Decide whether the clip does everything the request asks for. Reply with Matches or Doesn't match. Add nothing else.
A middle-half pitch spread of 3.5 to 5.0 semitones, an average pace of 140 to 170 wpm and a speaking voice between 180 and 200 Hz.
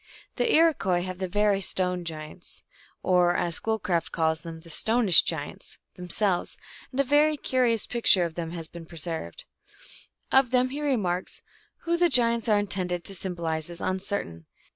Doesn't match